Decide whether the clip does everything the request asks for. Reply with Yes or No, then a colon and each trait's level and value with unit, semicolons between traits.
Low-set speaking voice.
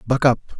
Yes: low, 125 Hz